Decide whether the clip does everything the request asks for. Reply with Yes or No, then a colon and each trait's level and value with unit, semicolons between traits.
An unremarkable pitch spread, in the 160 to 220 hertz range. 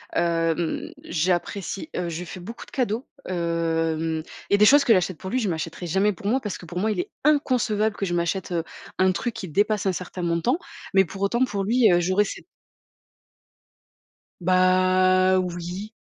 Yes: average, 3.4 semitones; medium, 185 Hz